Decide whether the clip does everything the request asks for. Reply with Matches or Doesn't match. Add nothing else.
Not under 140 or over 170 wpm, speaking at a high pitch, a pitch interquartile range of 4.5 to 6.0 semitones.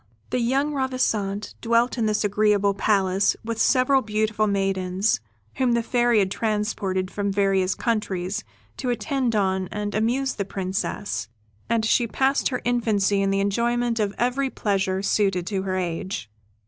Doesn't match